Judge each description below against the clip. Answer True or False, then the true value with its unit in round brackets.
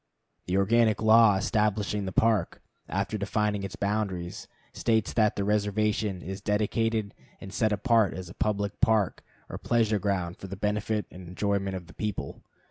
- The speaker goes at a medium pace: True (160 wpm)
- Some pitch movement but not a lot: False (1.9 semitones)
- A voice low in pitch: True (105 Hz)